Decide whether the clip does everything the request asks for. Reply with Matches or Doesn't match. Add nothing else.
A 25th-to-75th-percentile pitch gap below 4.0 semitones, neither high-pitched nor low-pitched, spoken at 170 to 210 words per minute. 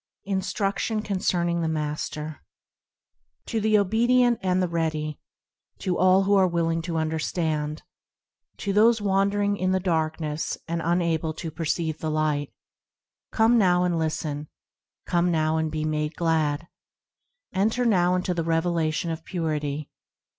Doesn't match